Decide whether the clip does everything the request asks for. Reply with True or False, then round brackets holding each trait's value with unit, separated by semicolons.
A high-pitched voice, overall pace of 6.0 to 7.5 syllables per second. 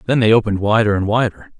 False (105 Hz; 7.3 syllables/s)